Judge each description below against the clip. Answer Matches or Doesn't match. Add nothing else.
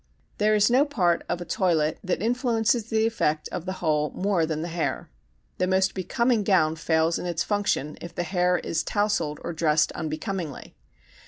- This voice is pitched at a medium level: Matches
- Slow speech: Doesn't match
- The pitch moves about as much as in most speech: Matches